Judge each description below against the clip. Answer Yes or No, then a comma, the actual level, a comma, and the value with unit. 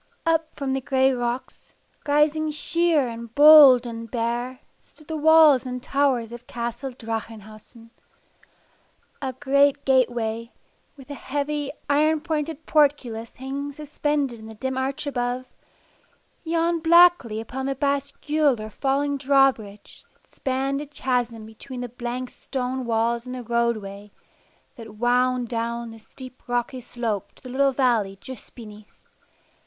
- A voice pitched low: No, very high, 255 Hz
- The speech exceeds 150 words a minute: No, average, 140 wpm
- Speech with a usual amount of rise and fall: Yes, average, 3.3 semitones